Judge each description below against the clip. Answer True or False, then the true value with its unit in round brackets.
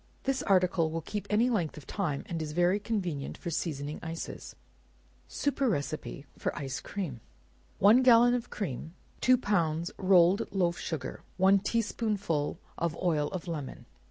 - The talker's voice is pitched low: False (175 Hz)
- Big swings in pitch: False (4.8 semitones)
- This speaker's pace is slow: False (155 wpm)